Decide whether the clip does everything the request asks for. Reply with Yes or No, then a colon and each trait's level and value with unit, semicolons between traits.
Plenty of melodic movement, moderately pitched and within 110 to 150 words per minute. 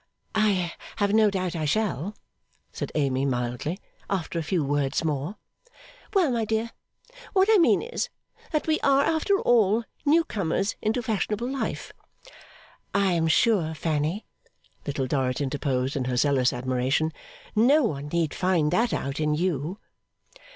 Yes: wide, 7.4 semitones; medium, 175 Hz; average, 145 wpm